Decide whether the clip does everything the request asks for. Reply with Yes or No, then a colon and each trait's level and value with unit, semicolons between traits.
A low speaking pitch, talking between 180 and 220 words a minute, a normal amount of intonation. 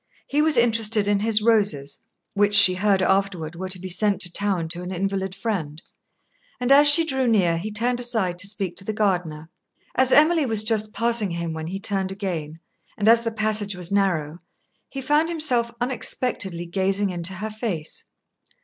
No: high, 200 Hz; average, 185 wpm; average, 4.1 semitones